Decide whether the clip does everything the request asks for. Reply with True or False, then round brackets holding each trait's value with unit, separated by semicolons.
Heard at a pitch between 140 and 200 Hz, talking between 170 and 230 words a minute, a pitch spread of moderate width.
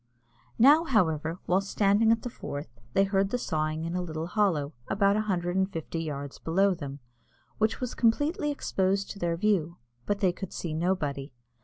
True (185 Hz; 180 wpm; 4.2 semitones)